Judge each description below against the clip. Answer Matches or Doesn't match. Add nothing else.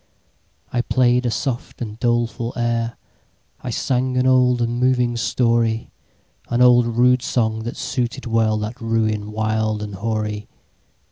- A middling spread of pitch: Doesn't match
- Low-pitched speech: Matches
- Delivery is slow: Matches